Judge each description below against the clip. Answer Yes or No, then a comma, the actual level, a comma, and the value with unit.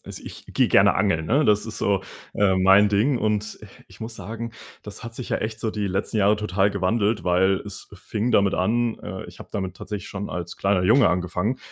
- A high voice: No, low, 105 Hz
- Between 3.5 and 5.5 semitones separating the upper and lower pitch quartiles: No, narrow, 2.6 semitones